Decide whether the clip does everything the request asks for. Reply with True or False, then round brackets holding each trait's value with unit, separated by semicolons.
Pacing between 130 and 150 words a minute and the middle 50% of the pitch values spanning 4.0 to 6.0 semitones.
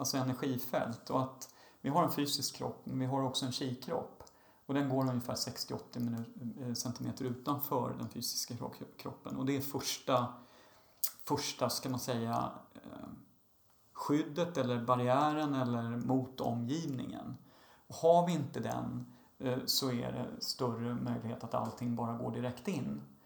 False (140 wpm; 2.4 semitones)